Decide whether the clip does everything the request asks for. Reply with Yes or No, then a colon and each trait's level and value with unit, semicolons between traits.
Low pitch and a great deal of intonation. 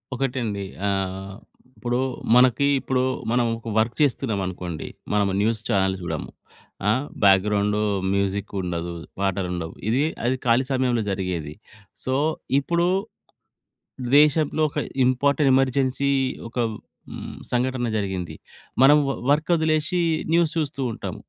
Yes: low, 120 Hz; wide, 5.7 semitones